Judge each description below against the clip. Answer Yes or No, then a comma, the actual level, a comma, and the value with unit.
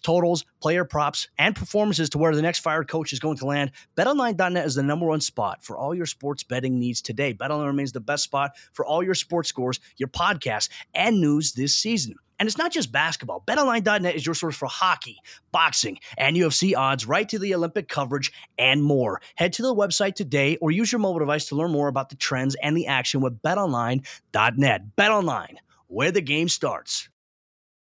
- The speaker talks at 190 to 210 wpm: Yes, average, 200 wpm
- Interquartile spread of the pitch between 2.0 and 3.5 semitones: No, average, 4.2 semitones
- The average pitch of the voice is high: No, medium, 155 Hz